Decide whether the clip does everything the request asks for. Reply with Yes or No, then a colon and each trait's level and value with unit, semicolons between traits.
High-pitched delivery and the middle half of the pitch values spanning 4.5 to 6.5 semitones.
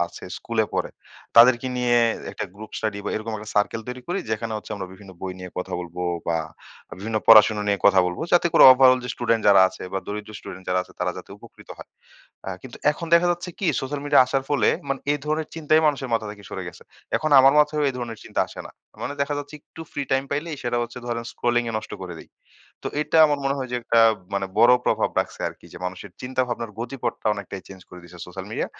No: low, 120 Hz; average, 5.1 semitones